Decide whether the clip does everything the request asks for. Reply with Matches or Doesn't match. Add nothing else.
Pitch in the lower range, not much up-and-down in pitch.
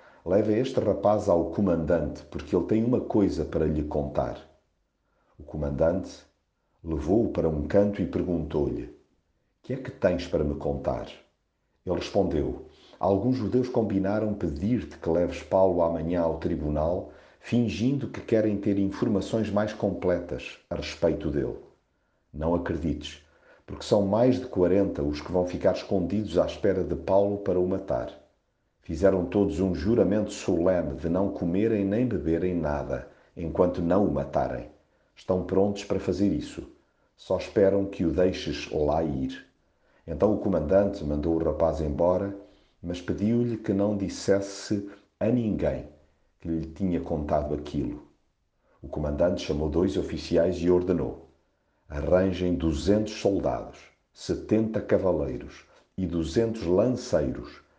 Doesn't match